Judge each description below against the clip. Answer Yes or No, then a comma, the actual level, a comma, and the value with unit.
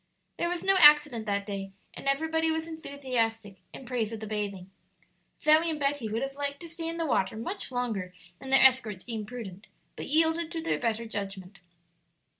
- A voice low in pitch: No, very high, 255 Hz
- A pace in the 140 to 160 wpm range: No, average, 190 wpm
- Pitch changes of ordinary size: No, wide, 6.8 semitones